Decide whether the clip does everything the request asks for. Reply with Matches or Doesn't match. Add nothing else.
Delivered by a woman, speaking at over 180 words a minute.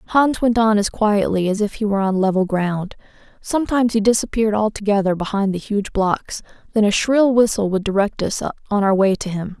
Matches